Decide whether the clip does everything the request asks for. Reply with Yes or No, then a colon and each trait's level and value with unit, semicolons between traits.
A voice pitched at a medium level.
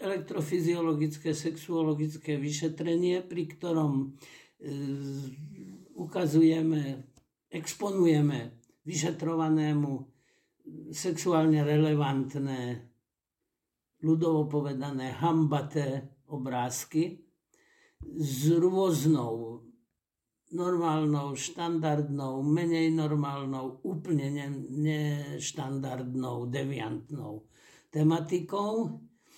Yes: medium, 150 Hz